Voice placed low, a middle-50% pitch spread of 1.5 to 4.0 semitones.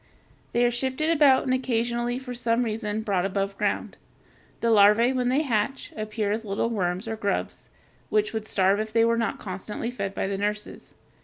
No: high, 225 Hz; average, 2.9 semitones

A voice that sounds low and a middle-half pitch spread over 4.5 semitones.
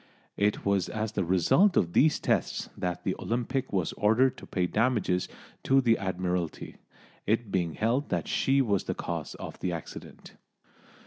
Yes: low, 100 Hz; average, 5.1 semitones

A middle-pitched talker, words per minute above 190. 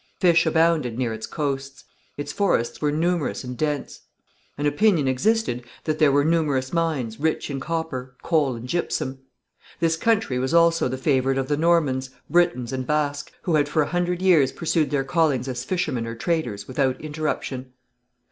No: medium, 145 Hz; average, 170 wpm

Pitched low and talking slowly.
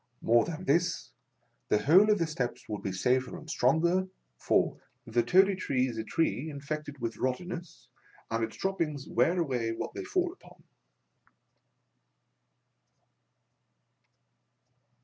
No: medium, 150 Hz; slow, 130 wpm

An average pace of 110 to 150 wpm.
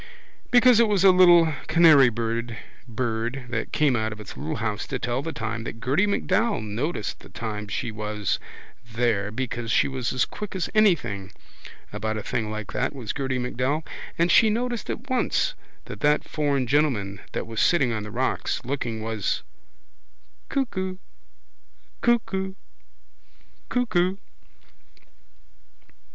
Yes: average, 140 wpm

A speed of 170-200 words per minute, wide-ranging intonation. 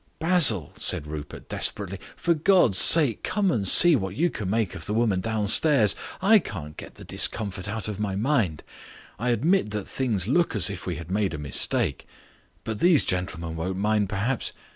Yes: average, 185 wpm; wide, 6.4 semitones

